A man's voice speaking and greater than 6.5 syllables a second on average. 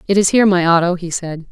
No: female; 6.8 syllables/s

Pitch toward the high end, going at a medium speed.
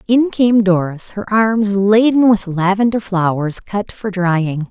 Yes: high, 200 Hz; average, 155 wpm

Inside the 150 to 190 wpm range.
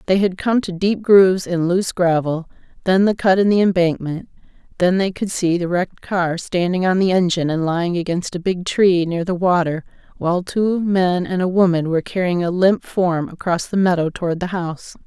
No: fast, 205 wpm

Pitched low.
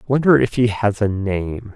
Yes: low, 110 Hz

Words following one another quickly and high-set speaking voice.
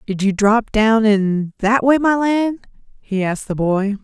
No: average, 195 wpm; high, 220 Hz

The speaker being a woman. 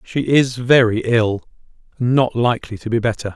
No: male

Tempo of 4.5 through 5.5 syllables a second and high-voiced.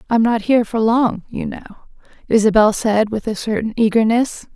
Yes: 5.4 syllables/s; high, 220 Hz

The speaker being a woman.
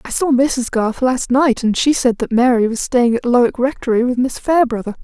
Yes: female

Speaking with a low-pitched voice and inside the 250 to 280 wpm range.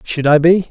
No: medium, 160 Hz; fast, 255 wpm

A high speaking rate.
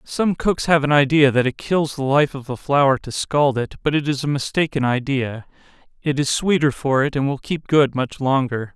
Yes: fast, 220 wpm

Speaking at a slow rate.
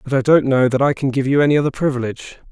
No: fast, 285 wpm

